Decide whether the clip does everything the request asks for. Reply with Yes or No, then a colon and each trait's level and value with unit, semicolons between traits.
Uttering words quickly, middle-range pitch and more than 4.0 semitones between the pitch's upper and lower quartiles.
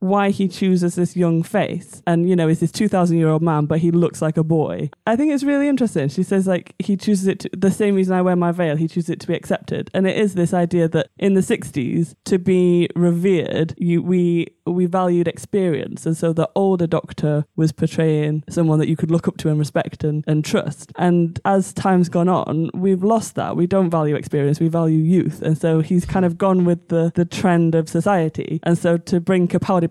No: fast, 230 wpm; medium, 175 Hz; narrow, 2.5 semitones